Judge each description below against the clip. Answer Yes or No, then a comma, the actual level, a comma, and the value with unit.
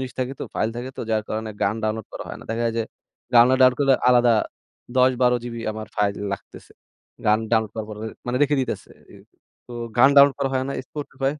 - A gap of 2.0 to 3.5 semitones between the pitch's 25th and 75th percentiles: Yes, average, 2.9 semitones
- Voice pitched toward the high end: No, low, 120 Hz